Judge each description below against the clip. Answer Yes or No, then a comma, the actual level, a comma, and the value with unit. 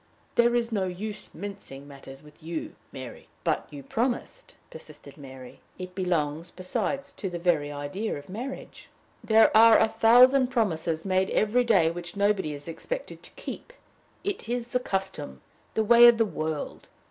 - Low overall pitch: No, high, 190 Hz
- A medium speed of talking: Yes, average, 160 wpm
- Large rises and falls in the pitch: Yes, wide, 6.7 semitones